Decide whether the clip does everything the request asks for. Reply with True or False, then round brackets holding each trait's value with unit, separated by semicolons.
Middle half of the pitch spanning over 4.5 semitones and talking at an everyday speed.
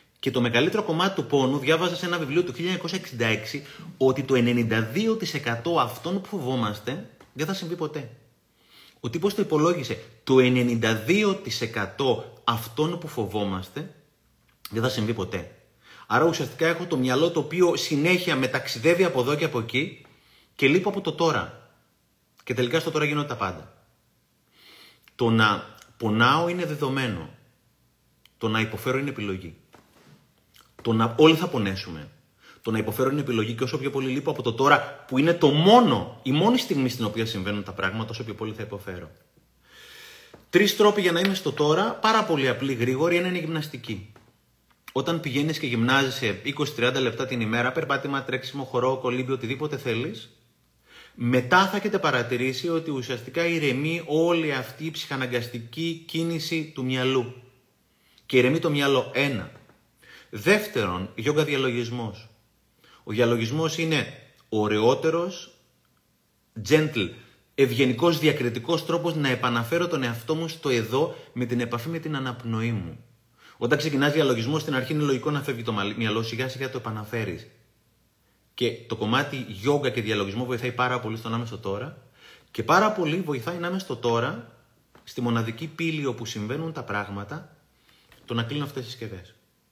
True (5.3 semitones; 150 wpm)